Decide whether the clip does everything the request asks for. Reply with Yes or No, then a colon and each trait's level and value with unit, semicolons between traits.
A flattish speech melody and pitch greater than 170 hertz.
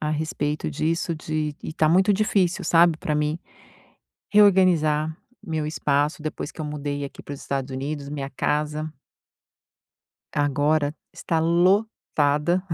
No: narrow, 2.3 semitones; medium, 155 Hz